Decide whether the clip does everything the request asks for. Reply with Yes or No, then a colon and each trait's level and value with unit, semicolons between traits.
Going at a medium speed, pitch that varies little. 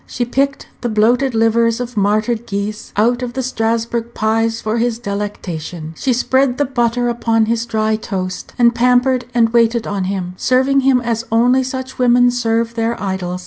Yes: average, 175 wpm; narrow, 2.1 semitones